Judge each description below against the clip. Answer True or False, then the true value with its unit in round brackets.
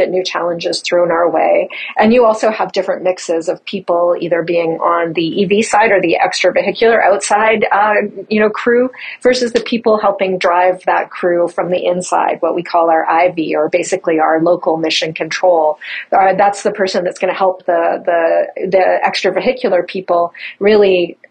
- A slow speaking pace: False (175 wpm)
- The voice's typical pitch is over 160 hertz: True (185 Hz)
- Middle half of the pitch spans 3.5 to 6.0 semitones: False (2.8 semitones)